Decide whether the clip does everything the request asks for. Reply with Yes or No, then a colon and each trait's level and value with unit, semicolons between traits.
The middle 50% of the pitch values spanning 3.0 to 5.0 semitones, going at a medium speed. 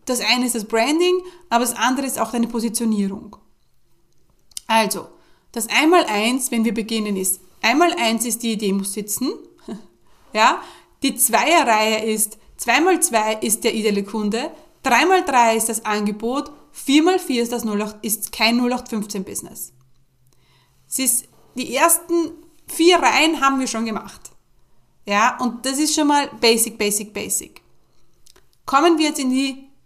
Yes: average, 4.4 semitones; average, 160 wpm